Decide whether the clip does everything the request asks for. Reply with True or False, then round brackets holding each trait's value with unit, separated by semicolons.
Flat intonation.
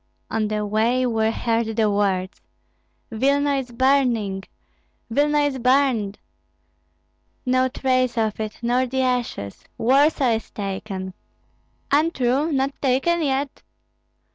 False (3.8 semitones)